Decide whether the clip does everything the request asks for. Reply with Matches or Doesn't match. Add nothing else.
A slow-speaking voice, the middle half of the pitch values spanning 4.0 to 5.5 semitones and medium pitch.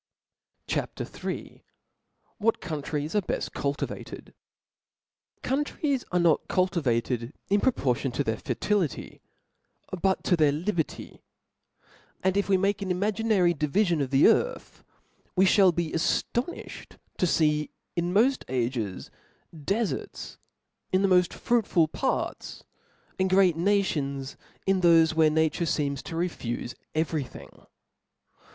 Matches